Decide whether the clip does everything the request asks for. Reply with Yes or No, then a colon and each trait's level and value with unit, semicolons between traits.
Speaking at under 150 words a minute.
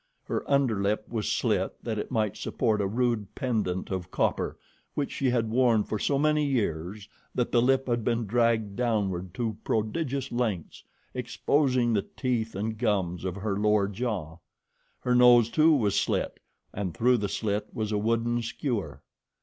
No: average, 165 wpm